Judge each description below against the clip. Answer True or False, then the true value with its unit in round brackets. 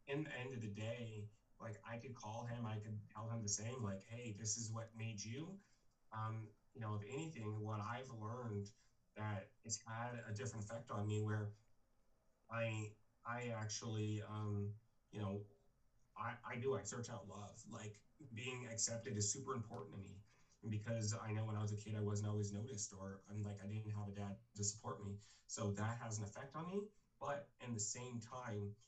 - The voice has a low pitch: True (110 Hz)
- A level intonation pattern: True (2.1 semitones)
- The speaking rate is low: False (200 wpm)